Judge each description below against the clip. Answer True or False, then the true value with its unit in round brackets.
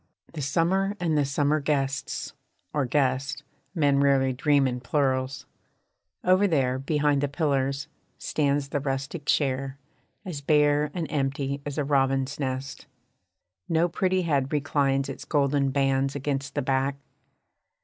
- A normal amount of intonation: False (1.6 semitones)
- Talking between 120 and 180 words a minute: True (135 wpm)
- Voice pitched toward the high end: False (140 Hz)